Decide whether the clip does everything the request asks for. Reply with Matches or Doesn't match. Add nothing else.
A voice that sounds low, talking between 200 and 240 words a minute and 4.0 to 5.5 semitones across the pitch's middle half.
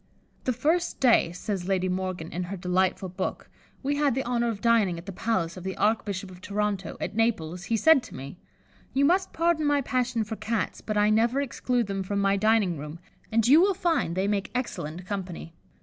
Doesn't match